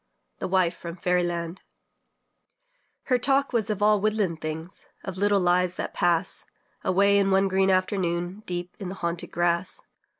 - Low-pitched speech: No, medium, 185 Hz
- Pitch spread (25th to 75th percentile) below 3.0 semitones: Yes, narrow, 2.5 semitones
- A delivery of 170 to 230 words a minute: No, average, 160 wpm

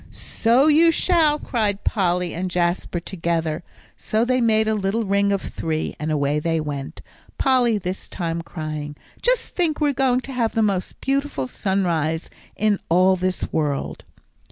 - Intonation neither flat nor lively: No, wide, 6.6 semitones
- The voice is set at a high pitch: Yes, high, 195 Hz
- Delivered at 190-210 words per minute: No, average, 155 wpm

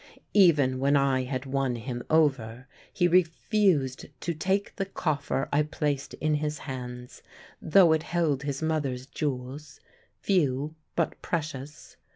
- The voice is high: No, medium, 145 Hz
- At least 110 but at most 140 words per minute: Yes, slow, 135 wpm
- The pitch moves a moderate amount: Yes, average, 3.4 semitones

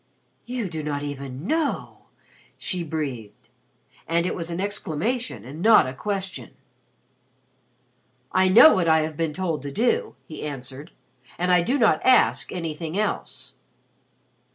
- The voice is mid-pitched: Yes, medium, 170 Hz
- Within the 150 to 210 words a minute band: No, slow, 135 wpm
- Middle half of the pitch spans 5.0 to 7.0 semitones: Yes, wide, 5.6 semitones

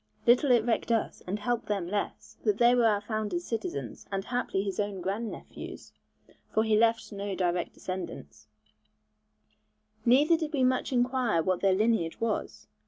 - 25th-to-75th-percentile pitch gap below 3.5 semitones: No, average, 3.8 semitones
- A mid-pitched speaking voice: No, high, 220 Hz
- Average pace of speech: Yes, average, 165 wpm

